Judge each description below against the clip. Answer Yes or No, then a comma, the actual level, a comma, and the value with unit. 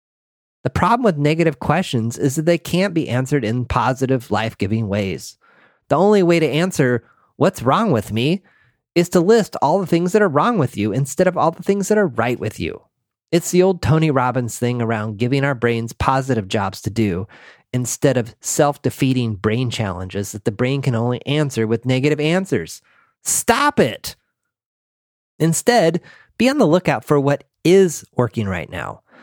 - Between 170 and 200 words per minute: Yes, average, 180 wpm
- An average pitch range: No, wide, 6.8 semitones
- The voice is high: No, low, 135 Hz